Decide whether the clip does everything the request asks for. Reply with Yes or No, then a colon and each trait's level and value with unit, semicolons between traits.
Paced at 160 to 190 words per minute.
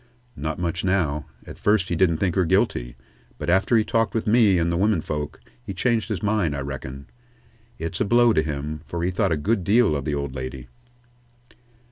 No: fast, 205 wpm